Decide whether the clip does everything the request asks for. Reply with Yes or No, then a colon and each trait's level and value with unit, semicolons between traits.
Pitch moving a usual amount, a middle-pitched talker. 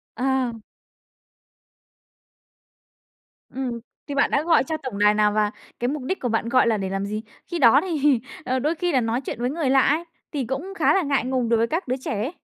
No: average, 4.0 semitones; very high, 260 Hz